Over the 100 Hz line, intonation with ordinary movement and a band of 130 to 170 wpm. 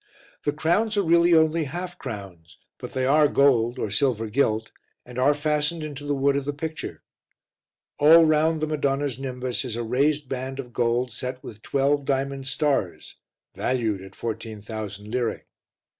Yes: low, 135 Hz; average, 4.2 semitones; average, 160 wpm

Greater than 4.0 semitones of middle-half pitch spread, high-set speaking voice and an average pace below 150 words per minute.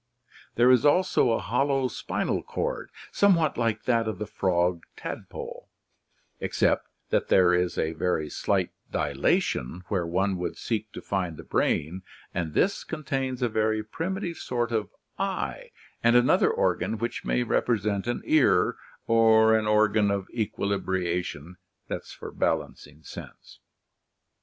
No: average, 5.1 semitones; low, 110 Hz; slow, 135 wpm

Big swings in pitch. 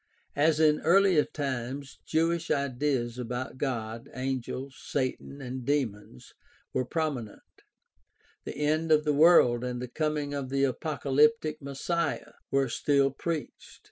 No: average, 3.2 semitones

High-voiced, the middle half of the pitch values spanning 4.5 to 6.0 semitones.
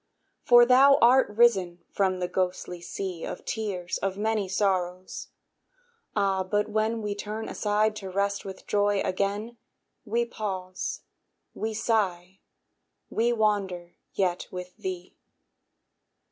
No: high, 200 Hz; average, 2.8 semitones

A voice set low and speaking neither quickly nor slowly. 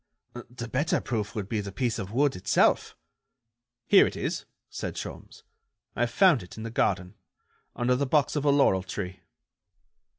Yes: low, 115 Hz; average, 165 wpm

